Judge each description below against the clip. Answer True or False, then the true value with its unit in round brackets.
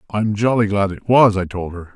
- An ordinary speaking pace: False (245 wpm)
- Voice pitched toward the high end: False (105 Hz)